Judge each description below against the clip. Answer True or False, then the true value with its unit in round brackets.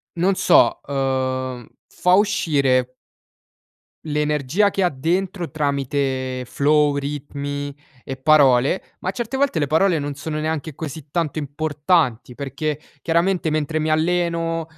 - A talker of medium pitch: True (150 Hz)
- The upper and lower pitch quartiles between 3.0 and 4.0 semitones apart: True (3.4 semitones)